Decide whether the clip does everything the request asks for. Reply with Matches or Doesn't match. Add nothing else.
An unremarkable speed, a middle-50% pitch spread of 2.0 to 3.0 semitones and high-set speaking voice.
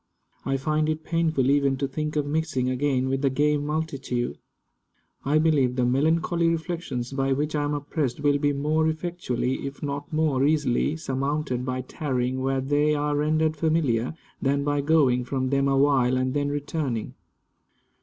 Doesn't match